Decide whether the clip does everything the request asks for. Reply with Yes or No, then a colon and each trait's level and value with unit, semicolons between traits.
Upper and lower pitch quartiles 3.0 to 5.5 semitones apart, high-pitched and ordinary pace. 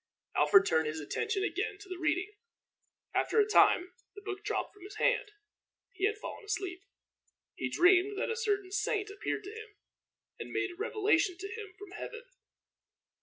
No: narrow, 2.4 semitones; very high, 405 Hz; average, 170 wpm